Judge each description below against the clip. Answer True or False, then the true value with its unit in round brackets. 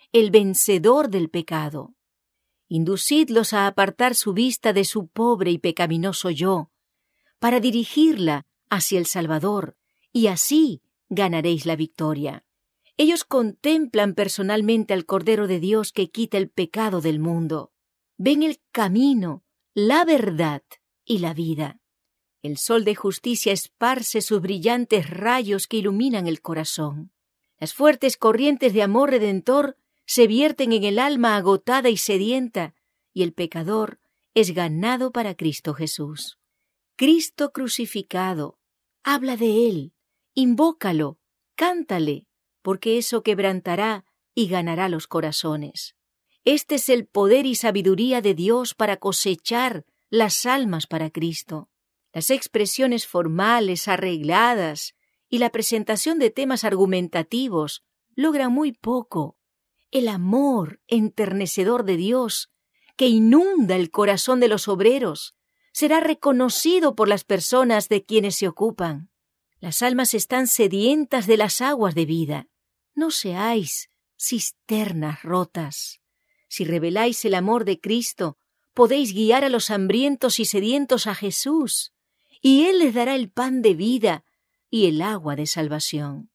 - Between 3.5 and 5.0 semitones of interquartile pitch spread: False (5.6 semitones)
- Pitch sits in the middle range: False (215 Hz)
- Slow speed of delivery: True (125 wpm)